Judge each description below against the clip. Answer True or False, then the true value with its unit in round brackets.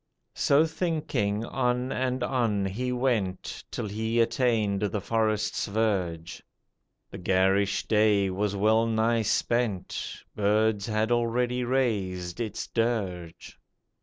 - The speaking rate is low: True (110 wpm)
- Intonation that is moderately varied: True (3.2 semitones)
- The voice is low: True (110 Hz)